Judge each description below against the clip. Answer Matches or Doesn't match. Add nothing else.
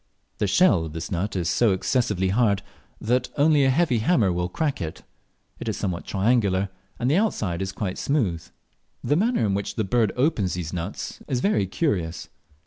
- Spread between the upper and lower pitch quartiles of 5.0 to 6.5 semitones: Matches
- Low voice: Matches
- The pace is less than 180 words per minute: Doesn't match